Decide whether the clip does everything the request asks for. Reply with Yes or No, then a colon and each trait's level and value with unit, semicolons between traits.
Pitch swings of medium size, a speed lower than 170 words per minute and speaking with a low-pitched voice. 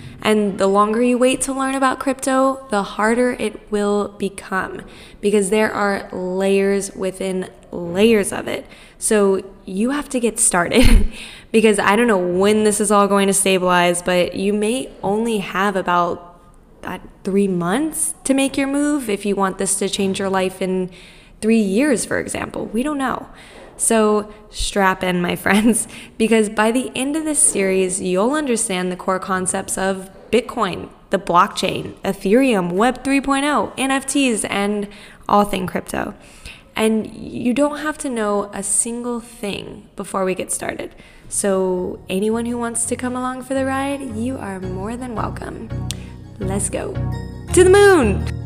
No: average, 4.2 semitones; average, 160 wpm; high, 210 Hz